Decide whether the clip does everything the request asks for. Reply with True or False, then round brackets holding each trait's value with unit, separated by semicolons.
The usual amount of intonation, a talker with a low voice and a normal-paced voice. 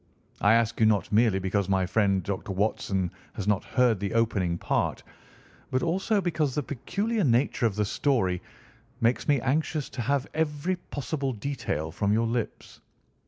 False (6.1 semitones; 115 Hz; 165 wpm)